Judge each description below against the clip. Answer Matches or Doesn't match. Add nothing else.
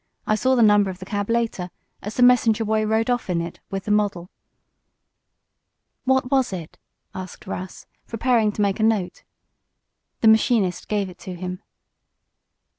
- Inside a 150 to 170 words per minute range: Matches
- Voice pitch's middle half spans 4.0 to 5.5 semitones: Doesn't match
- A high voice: Matches